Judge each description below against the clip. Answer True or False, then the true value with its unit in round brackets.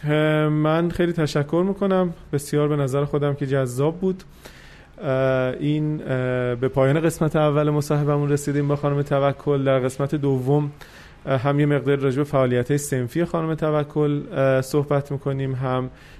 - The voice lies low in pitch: False (145 Hz)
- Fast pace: False (135 wpm)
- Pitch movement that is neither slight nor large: False (1.9 semitones)